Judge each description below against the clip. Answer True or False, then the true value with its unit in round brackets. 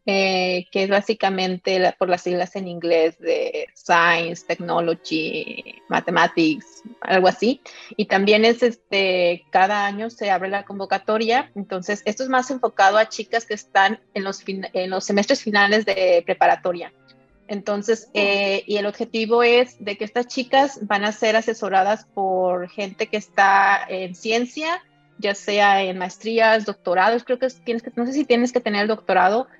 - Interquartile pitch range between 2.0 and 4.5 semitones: True (3.5 semitones)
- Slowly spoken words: False (165 wpm)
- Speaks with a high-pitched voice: True (205 Hz)